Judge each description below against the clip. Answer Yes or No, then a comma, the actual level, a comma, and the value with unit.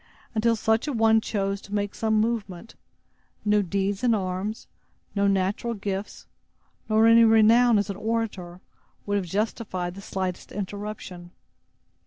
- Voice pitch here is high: Yes, high, 205 Hz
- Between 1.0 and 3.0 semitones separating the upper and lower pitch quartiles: Yes, narrow, 2.4 semitones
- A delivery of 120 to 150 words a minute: Yes, average, 140 wpm